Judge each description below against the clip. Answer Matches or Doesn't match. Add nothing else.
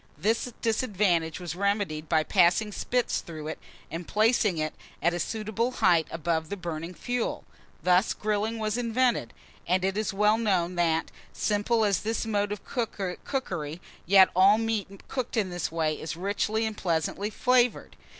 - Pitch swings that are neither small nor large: Matches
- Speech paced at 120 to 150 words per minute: Doesn't match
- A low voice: Doesn't match